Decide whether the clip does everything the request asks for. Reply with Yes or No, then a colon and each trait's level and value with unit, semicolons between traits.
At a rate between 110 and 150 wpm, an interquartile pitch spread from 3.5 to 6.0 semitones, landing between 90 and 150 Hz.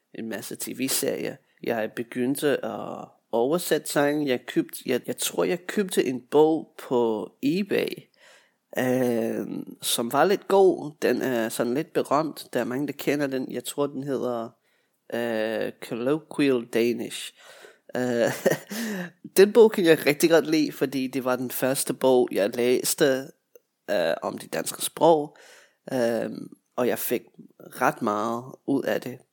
Yes: slow, 145 wpm; average, 4.3 semitones; low, 135 Hz